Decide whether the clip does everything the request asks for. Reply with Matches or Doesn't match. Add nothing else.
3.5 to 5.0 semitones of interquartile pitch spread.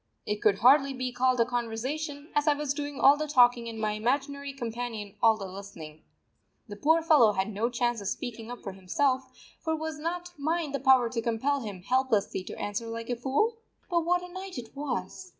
Matches